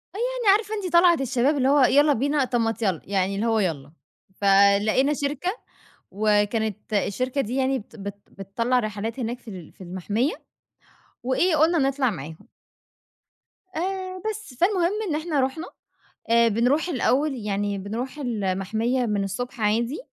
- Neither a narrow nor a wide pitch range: No, wide, 6.1 semitones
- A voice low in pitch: No, high, 245 Hz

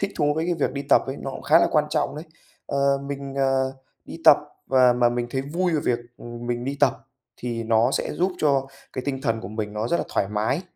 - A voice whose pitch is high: No, low, 135 Hz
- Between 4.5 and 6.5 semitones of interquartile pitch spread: No, average, 3.4 semitones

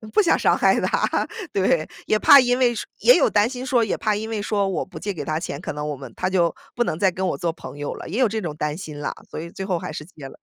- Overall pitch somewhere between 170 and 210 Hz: Yes, high, 190 Hz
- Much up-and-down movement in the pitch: Yes, wide, 6.1 semitones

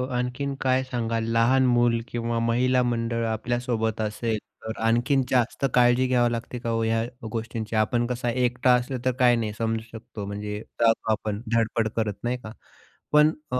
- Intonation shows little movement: Yes, narrow, 1.7 semitones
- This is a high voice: No, low, 115 Hz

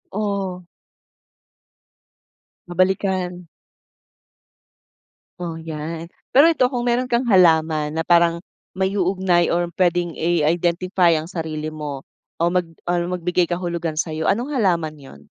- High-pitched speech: No, medium, 175 Hz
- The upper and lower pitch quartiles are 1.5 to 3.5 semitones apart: Yes, narrow, 2.5 semitones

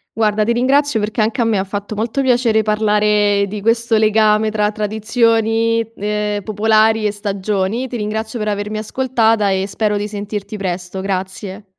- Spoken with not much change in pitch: Yes, narrow, 1.6 semitones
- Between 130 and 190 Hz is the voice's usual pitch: No, high, 215 Hz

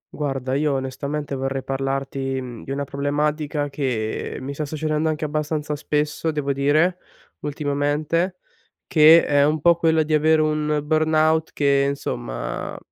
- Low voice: No, medium, 150 Hz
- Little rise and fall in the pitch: Yes, narrow, 2.0 semitones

